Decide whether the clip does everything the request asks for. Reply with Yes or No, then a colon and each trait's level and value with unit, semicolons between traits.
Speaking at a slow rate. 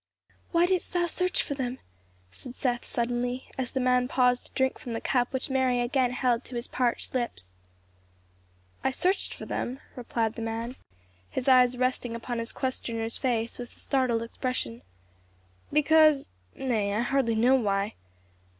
No: average, 160 wpm